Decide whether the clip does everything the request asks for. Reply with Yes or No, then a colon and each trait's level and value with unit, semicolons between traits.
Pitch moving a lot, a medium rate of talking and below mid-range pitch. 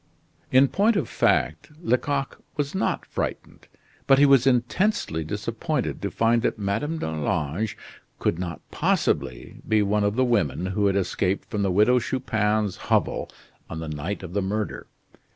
Yes: wide, 5.7 semitones; average, 155 wpm; low, 105 Hz